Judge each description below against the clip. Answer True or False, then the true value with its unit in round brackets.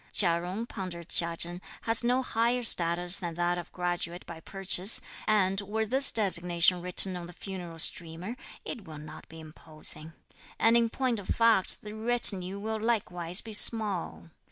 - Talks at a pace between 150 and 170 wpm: True (165 wpm)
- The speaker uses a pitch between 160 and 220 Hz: True (185 Hz)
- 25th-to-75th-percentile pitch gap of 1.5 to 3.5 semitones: False (4.3 semitones)